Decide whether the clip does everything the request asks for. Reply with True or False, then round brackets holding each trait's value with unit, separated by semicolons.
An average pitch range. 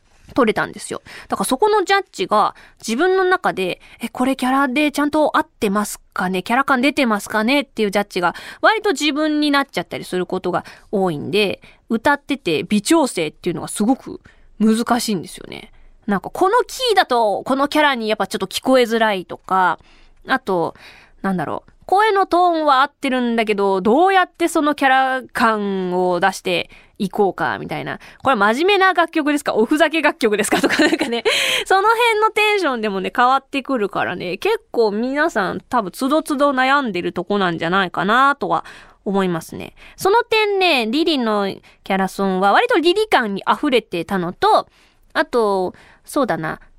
False (7.8 semitones)